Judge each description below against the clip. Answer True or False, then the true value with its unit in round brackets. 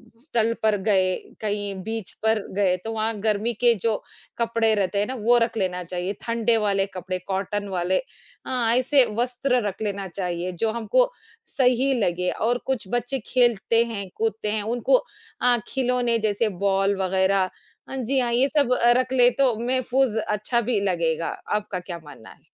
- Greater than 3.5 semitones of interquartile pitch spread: True (3.9 semitones)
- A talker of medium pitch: False (220 Hz)